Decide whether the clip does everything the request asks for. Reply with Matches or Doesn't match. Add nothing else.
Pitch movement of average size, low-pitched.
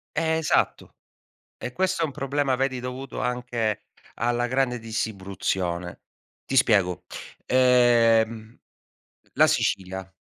Matches